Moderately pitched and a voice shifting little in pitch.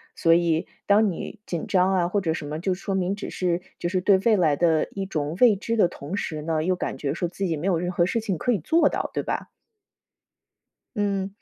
No: medium, 180 Hz; average, 3.2 semitones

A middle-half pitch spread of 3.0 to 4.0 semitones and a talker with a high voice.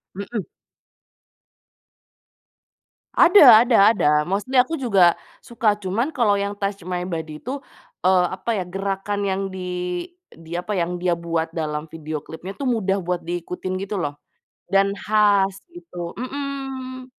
No: average, 4.8 semitones; high, 195 Hz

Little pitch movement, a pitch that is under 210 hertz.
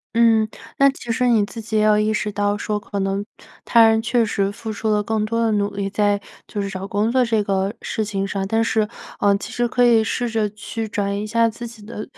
No: narrow, 2.0 semitones; high, 215 Hz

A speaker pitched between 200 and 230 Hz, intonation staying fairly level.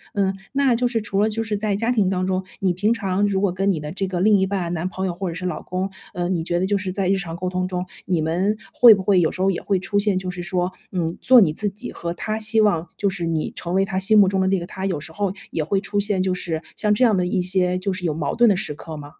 No: high, 190 Hz; narrow, 2.3 semitones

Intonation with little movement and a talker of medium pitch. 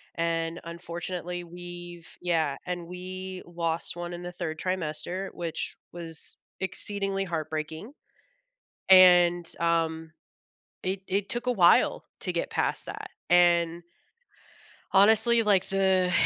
Yes: narrow, 2.0 semitones; medium, 175 Hz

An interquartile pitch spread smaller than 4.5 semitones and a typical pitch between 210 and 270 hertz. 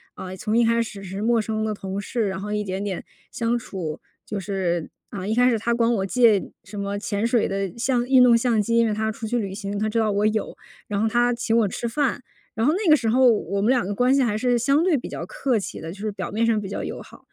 Yes: average, 3.1 semitones; high, 220 Hz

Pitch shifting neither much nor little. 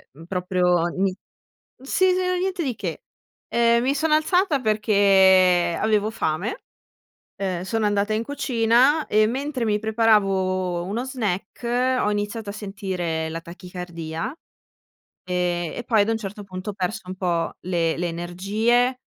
Yes: average, 4.6 semitones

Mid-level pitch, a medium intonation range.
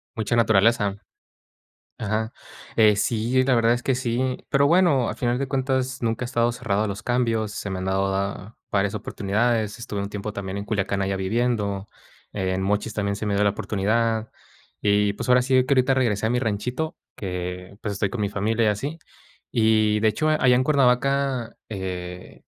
No: low, 110 Hz; average, 3.6 semitones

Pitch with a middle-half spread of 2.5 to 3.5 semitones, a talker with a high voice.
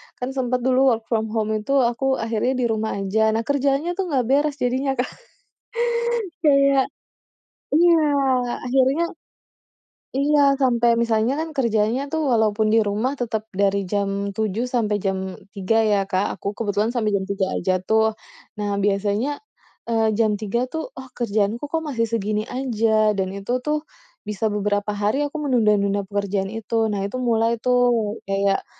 No: average, 4.0 semitones; high, 225 Hz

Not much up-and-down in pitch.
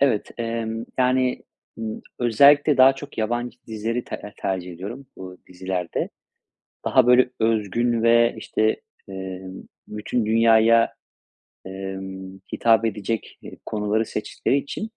No: average, 3.6 semitones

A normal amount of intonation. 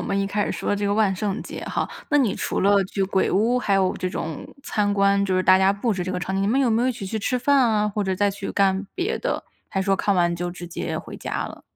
No: narrow, 2.0 semitones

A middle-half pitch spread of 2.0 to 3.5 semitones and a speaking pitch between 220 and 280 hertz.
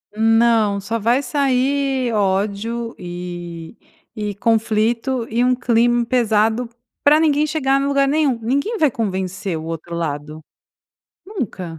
No: average, 5.2 semitones; high, 230 Hz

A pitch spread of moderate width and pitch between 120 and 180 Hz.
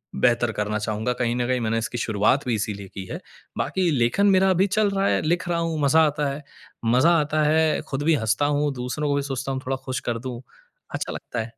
Yes: average, 5.0 semitones; low, 135 Hz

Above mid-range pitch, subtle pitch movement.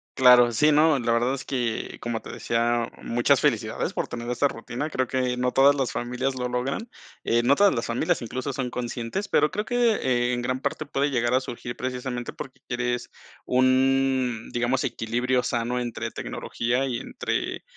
No: low, 125 Hz; narrow, 1.9 semitones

